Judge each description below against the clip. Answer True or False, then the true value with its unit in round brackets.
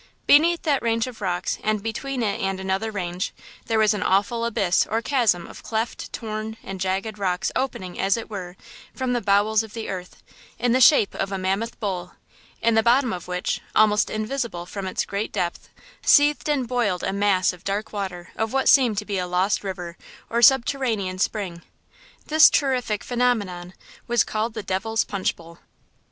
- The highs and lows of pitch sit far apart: False (3.8 semitones)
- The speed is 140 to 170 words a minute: False (185 wpm)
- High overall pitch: True (215 Hz)